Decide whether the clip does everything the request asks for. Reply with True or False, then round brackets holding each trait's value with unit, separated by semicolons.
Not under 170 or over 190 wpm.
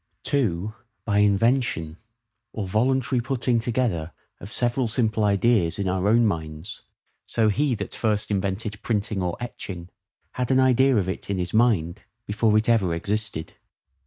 False (150 wpm)